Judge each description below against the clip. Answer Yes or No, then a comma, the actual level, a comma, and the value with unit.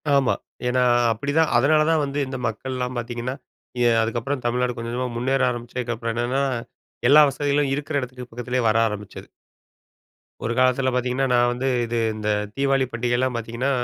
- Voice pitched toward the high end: No, low, 125 Hz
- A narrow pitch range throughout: Yes, narrow, 2.3 semitones